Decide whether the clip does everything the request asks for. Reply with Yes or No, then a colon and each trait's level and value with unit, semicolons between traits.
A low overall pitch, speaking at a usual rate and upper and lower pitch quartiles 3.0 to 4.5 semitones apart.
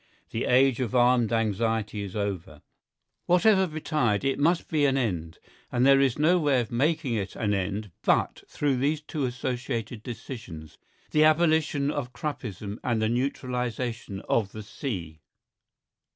No: low, 125 Hz; average, 150 wpm; average, 4.9 semitones